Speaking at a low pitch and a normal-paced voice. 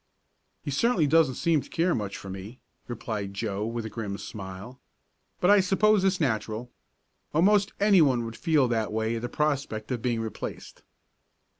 Yes: low, 120 Hz; average, 165 wpm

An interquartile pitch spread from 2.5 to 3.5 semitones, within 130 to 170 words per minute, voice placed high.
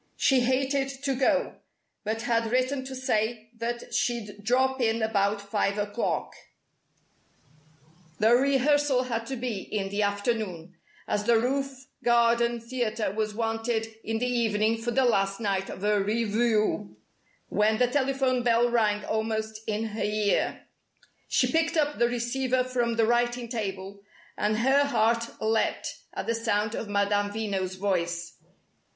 Yes: average, 3.0 semitones; average, 145 wpm; high, 225 Hz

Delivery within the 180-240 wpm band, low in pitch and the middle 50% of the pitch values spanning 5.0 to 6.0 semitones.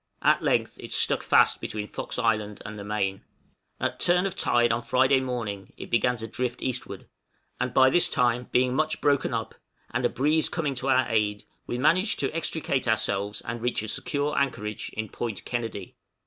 No: average, 190 wpm; low, 120 Hz; average, 4.0 semitones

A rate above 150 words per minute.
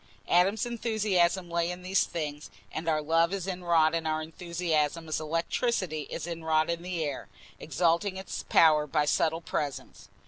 Yes: average, 165 wpm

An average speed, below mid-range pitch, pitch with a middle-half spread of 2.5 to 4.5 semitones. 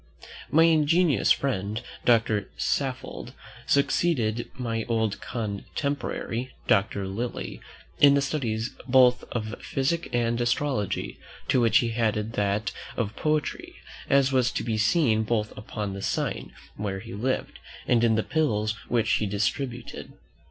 No: slow, 130 wpm; low, 115 Hz; average, 3.8 semitones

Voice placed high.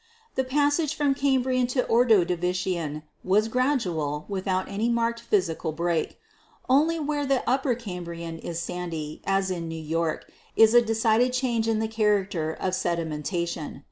Yes: high, 200 Hz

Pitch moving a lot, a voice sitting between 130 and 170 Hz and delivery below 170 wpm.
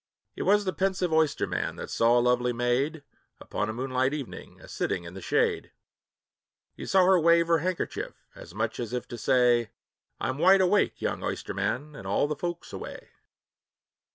No: wide, 6.0 semitones; low, 135 Hz; average, 180 wpm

